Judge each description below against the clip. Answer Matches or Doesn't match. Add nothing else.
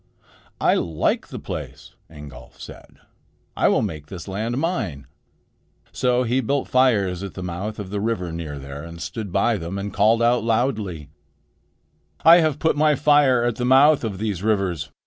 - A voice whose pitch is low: Matches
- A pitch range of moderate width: Doesn't match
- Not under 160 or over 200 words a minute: Matches